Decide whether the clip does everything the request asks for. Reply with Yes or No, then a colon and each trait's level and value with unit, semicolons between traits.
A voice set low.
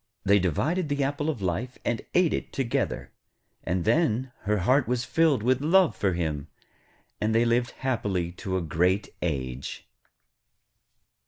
Yes: low, 115 Hz